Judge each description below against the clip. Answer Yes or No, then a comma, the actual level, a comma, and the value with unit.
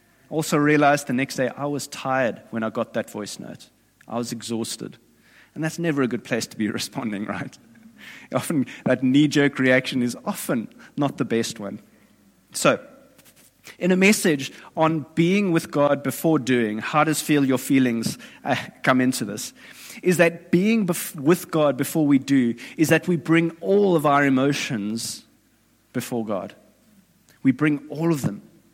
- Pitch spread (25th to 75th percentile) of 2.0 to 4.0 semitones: No, average, 4.6 semitones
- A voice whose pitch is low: No, medium, 145 Hz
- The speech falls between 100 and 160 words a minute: No, average, 170 wpm